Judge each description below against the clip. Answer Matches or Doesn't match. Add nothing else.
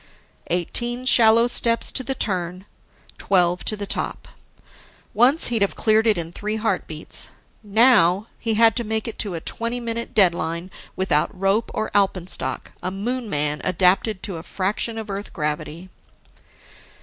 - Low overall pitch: Doesn't match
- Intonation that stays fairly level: Doesn't match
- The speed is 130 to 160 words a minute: Matches